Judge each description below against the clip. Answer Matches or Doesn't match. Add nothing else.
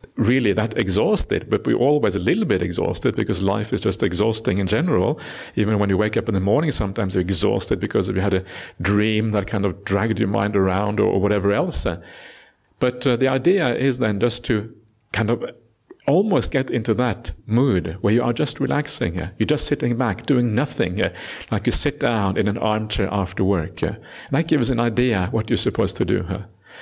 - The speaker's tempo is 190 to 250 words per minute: Matches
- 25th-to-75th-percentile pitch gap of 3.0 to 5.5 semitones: Matches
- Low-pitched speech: Matches